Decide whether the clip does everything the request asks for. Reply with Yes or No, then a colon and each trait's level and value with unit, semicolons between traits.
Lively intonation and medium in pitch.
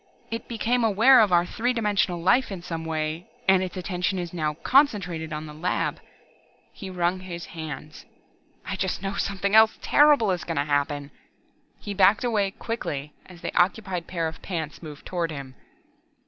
No: average, 4.3 semitones; medium, 180 Hz